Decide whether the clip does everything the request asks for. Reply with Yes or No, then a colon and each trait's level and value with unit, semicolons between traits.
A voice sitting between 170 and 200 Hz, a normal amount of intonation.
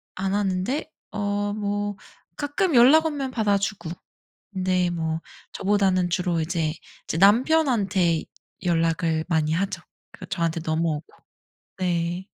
Yes: medium, 185 Hz; average, 3.6 semitones